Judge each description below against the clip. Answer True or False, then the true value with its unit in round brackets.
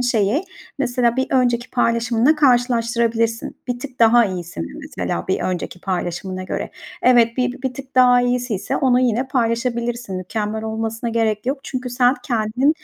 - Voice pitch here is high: True (235 Hz)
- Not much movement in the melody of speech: True (2.2 semitones)